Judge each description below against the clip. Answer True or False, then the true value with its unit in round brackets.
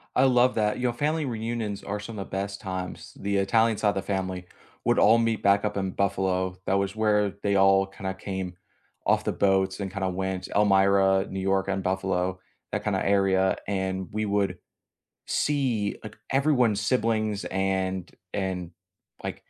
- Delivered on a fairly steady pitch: True (2.1 semitones)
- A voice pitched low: True (100 Hz)